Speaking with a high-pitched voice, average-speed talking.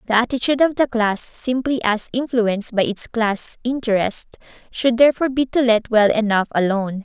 Yes: high, 230 Hz; average, 170 wpm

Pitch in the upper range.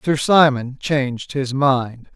No: low, 135 Hz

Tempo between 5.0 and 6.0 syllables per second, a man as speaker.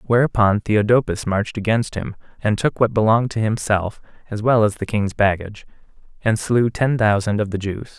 Yes: 5.3 syllables/s; male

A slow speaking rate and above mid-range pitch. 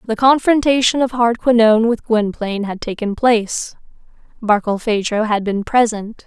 Yes: slow, 125 wpm; high, 225 Hz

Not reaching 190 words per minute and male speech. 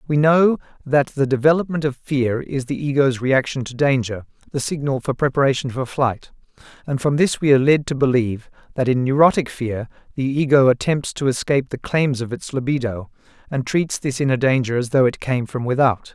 No: average, 195 wpm; male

